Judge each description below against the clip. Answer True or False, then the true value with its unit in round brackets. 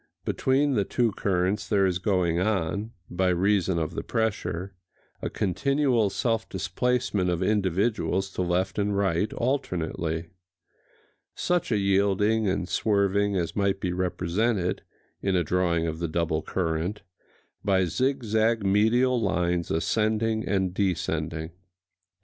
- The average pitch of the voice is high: False (95 Hz)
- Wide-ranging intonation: False (3.5 semitones)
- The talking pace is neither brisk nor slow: False (125 wpm)